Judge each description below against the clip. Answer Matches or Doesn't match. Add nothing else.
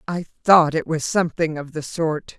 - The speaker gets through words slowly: Doesn't match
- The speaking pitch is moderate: Matches